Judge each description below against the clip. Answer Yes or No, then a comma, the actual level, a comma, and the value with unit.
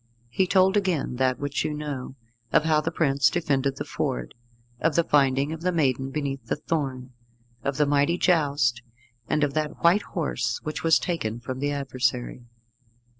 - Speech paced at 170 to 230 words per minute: Yes, average, 175 wpm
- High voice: No, medium, 145 Hz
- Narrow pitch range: No, average, 3.6 semitones